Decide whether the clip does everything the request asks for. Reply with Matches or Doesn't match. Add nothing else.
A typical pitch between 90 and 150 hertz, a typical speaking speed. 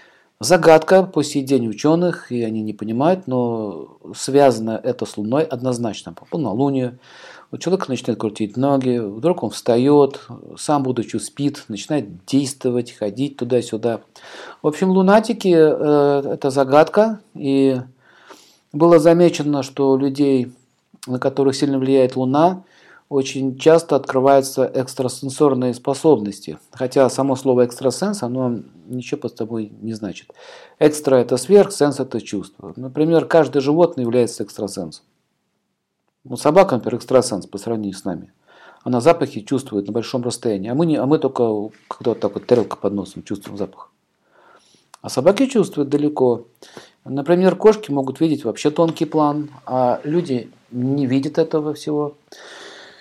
Matches